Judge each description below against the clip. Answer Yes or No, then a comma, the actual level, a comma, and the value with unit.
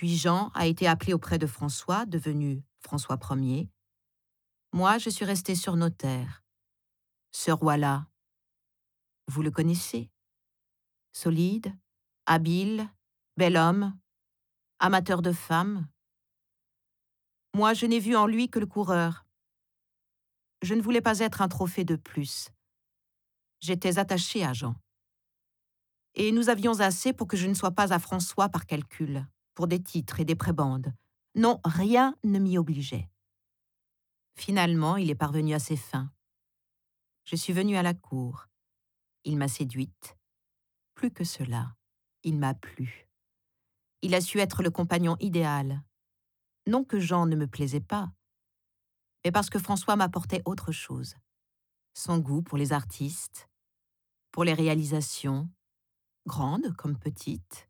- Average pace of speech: No, slow, 135 wpm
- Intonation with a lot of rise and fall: Yes, wide, 6.0 semitones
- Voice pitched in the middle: Yes, medium, 165 Hz